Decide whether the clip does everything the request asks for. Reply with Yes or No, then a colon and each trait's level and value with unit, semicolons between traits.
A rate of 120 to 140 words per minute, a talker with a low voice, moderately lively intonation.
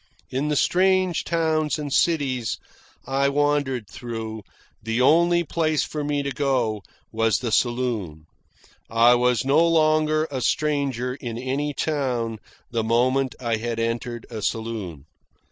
Yes: slow, 135 wpm; low, 130 Hz; average, 4.4 semitones